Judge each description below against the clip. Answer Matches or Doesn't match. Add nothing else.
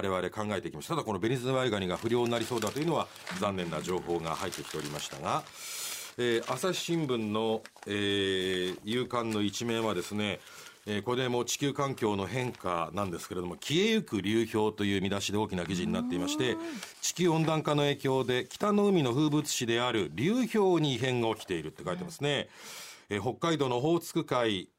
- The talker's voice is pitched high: Doesn't match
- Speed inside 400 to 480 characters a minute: Matches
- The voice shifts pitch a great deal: Matches